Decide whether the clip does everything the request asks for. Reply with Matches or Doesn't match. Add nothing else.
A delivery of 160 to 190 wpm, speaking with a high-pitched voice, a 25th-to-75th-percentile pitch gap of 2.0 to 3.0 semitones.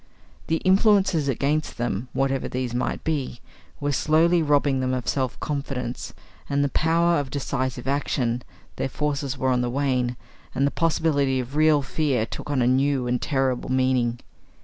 Doesn't match